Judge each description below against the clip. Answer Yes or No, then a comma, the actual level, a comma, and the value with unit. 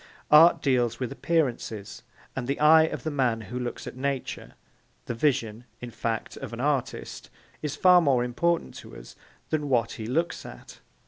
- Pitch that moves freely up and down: No, average, 4.3 semitones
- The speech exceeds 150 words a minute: Yes, average, 175 wpm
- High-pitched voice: No, low, 130 Hz